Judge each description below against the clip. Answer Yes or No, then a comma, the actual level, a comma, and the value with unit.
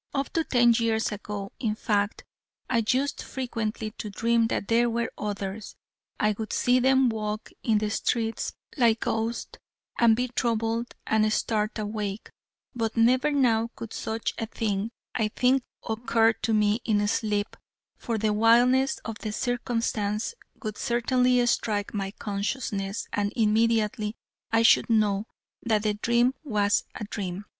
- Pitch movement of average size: No, narrow, 2.1 semitones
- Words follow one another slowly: No, average, 150 wpm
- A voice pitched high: Yes, high, 225 Hz